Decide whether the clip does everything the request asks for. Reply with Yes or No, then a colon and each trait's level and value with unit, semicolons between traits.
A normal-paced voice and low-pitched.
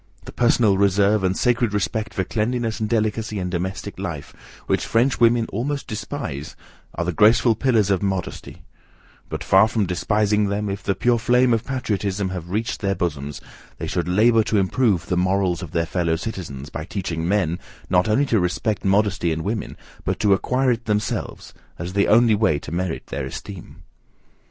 Yes: average, 180 wpm; low, 100 Hz